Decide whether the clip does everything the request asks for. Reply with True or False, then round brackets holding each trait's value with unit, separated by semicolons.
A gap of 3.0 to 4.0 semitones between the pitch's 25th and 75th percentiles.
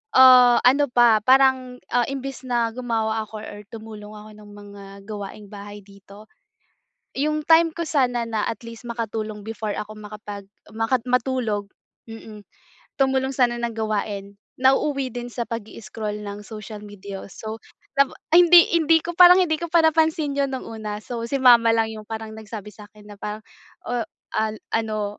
True (3.7 semitones)